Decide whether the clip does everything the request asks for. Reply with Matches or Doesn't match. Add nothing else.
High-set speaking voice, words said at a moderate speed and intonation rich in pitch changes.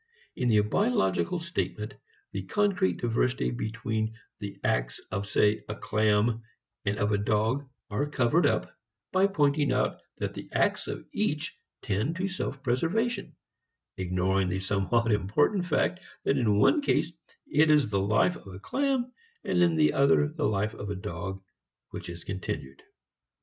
Doesn't match